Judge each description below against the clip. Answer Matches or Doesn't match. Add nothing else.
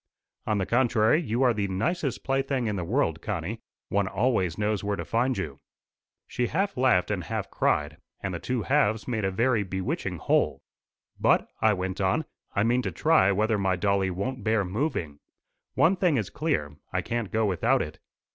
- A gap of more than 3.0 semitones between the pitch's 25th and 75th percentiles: Matches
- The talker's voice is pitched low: Matches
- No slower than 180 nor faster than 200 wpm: Matches